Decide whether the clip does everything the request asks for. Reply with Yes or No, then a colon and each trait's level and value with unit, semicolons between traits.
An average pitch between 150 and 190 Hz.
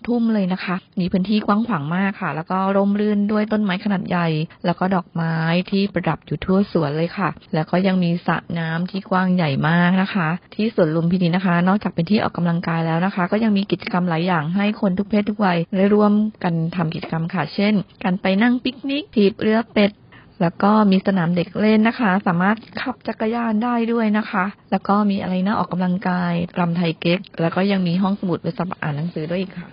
Yes: medium, 185 Hz